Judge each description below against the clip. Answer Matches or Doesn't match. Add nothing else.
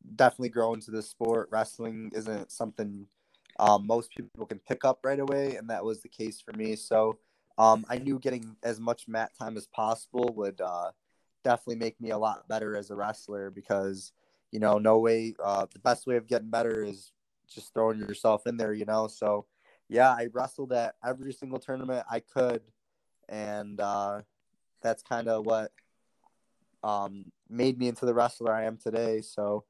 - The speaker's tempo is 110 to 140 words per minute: Doesn't match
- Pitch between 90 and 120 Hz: Matches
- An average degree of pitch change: Doesn't match